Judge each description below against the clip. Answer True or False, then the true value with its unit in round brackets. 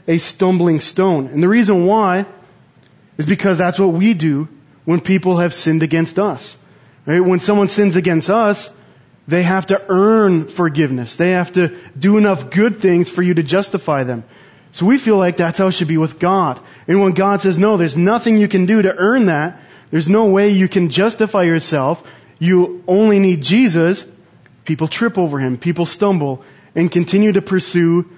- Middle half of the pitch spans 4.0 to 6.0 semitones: False (3.1 semitones)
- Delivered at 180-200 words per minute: True (185 wpm)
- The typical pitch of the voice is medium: True (180 Hz)